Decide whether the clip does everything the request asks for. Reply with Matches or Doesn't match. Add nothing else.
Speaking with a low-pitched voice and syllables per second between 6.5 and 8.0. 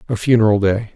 Matches